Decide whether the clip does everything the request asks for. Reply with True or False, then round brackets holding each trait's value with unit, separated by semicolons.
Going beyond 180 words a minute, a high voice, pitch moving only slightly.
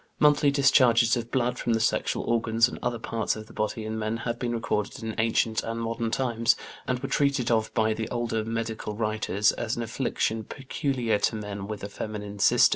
False (200 wpm; 115 Hz; 1.7 semitones)